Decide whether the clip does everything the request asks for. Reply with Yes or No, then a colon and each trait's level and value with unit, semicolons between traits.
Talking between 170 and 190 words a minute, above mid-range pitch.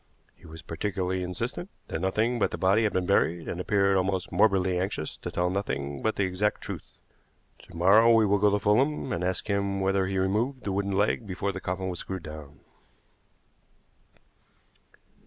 No: average, 180 wpm; very low, 95 Hz